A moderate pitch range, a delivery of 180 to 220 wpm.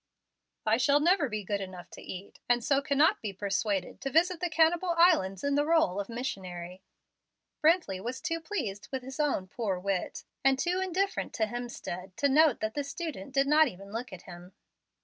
No: wide, 8.2 semitones; average, 190 wpm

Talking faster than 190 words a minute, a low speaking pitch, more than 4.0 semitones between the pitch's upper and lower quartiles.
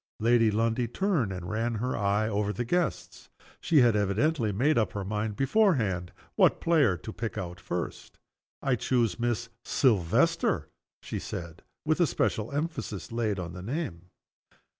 No: average, 155 wpm; low, 110 Hz; average, 4.4 semitones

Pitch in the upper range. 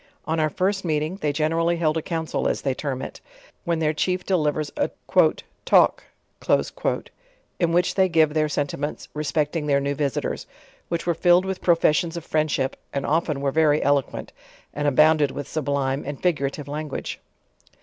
No: medium, 155 Hz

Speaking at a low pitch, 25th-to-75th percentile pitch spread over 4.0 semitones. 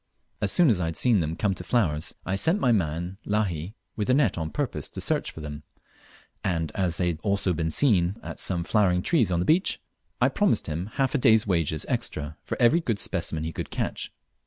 Yes: very low, 95 Hz; average, 5.2 semitones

